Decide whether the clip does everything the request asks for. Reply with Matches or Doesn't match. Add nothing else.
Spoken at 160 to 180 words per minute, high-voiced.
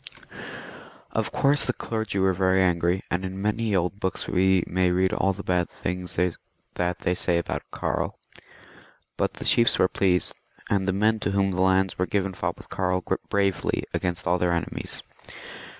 Doesn't match